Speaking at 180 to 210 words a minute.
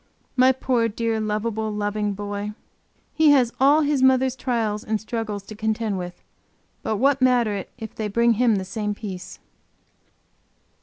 No: average, 155 wpm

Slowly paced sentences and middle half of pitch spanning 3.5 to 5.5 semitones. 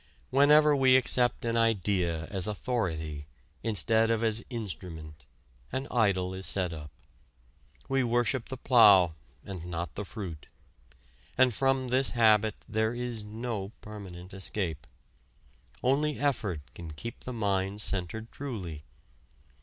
Yes: slow, 125 wpm; average, 5.1 semitones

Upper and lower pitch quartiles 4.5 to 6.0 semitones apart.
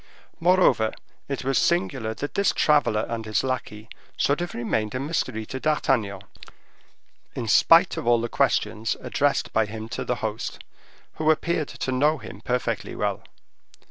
Yes: average, 5.2 semitones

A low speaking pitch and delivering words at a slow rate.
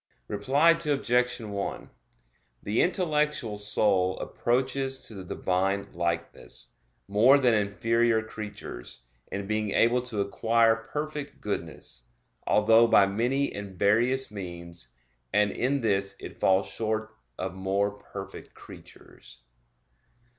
Yes: low, 110 Hz; slow, 110 wpm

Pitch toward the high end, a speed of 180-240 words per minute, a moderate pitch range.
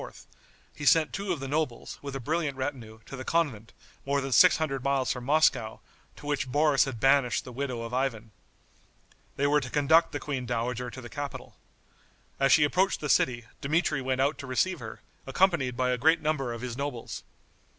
No: low, 135 Hz; average, 195 wpm; average, 3.0 semitones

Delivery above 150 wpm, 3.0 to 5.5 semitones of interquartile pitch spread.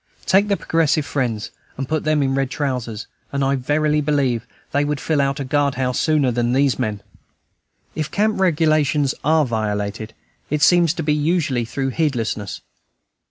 Yes: average, 160 wpm; average, 3.6 semitones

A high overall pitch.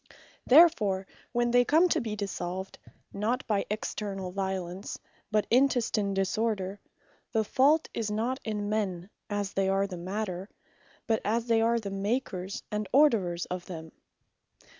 Yes: high, 210 Hz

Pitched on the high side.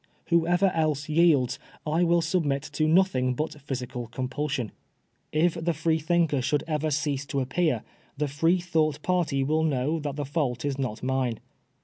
No: medium, 150 Hz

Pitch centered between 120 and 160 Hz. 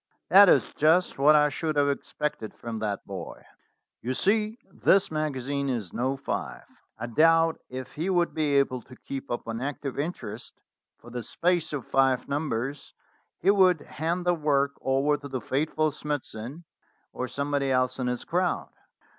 Yes: medium, 140 Hz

